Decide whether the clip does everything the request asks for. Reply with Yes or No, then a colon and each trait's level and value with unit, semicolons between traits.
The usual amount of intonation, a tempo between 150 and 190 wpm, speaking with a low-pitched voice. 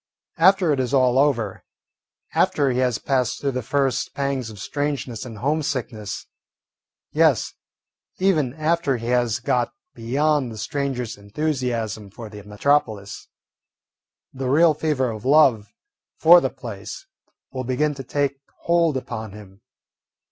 No: average, 4.2 semitones; slow, 135 wpm; low, 130 Hz